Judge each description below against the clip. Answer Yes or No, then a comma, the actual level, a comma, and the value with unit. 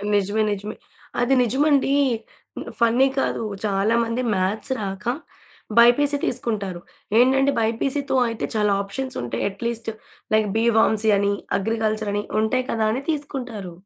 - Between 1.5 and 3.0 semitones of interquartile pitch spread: No, average, 4.0 semitones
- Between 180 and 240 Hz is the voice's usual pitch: Yes, high, 225 Hz